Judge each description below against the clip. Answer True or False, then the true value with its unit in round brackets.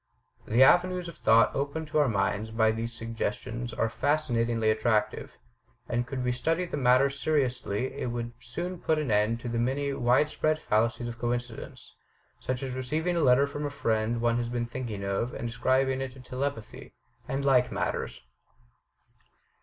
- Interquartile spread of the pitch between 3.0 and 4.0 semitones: True (3.3 semitones)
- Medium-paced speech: True (175 wpm)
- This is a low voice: True (125 Hz)